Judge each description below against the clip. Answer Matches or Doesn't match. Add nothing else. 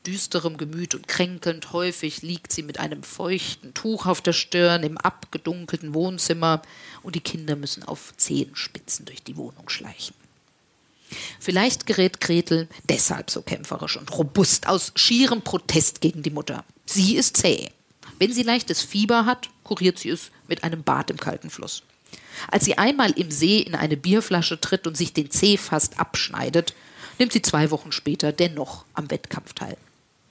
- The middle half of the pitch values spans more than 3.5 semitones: Doesn't match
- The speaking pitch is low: Doesn't match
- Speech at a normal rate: Matches